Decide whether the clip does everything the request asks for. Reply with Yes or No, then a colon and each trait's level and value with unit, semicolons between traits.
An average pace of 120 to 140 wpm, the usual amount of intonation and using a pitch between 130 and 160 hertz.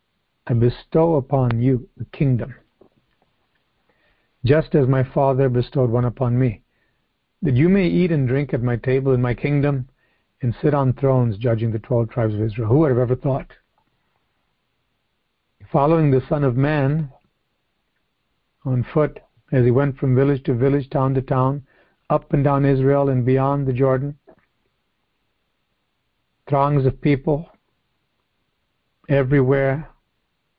No: slow, 135 wpm; narrow, 2.3 semitones; low, 135 Hz